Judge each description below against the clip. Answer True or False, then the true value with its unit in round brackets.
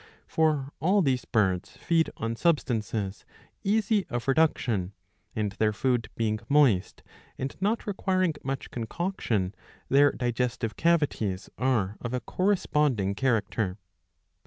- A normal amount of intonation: False (6.9 semitones)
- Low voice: True (125 Hz)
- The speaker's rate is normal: False (115 wpm)